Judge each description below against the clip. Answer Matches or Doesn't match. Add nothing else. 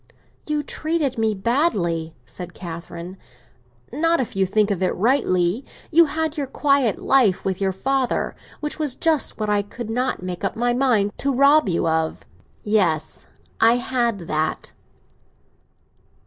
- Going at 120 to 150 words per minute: Matches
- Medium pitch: Doesn't match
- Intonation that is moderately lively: Doesn't match